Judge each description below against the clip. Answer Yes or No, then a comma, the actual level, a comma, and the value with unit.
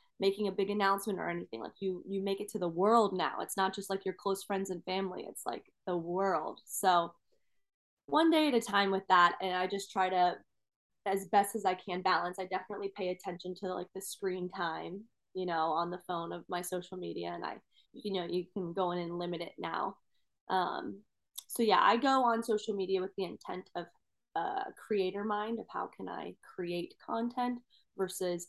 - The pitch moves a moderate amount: No, narrow, 2.1 semitones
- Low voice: No, high, 190 Hz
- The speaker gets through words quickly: Yes, fast, 210 wpm